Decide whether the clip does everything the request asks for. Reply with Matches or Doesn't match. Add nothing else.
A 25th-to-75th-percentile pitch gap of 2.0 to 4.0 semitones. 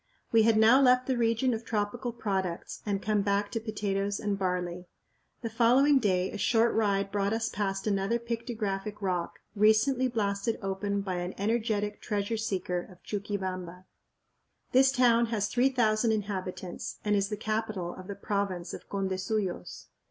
Matches